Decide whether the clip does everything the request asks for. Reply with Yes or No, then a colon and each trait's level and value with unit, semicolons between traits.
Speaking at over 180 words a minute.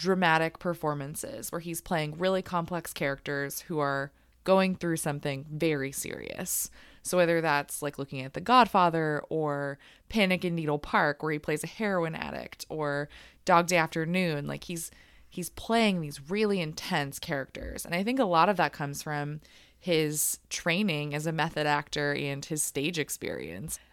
No: average, 165 wpm